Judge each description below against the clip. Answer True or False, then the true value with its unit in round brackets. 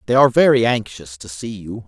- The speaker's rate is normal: False (225 wpm)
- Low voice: True (110 Hz)